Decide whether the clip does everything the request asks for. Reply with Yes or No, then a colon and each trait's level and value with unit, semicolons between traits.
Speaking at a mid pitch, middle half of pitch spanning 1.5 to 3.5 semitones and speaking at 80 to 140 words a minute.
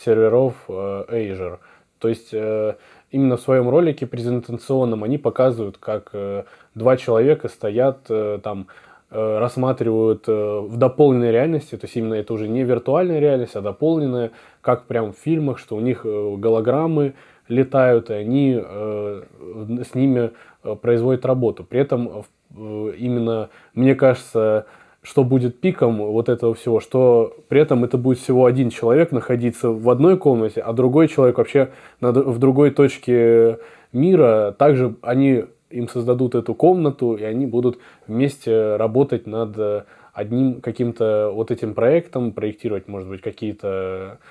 No: low, 120 Hz; average, 3.2 semitones; average, 130 wpm